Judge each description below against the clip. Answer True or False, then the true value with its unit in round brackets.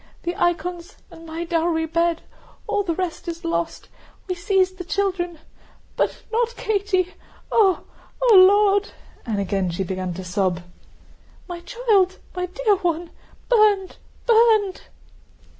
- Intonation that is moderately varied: True (3.6 semitones)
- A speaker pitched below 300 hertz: False (360 Hz)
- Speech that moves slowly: True (130 wpm)